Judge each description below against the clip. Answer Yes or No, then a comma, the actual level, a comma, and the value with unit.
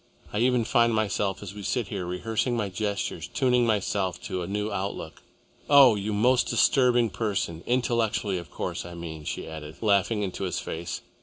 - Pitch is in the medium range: No, low, 105 Hz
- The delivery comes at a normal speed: Yes, average, 175 wpm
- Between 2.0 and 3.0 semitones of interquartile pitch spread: No, average, 4.1 semitones